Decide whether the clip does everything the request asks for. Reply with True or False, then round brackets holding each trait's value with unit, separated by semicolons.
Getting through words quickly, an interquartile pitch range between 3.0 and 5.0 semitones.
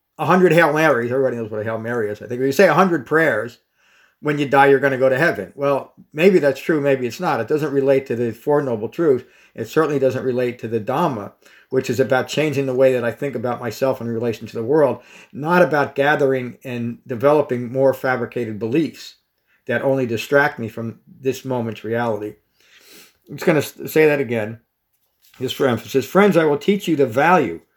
True (210 wpm; 3.6 semitones)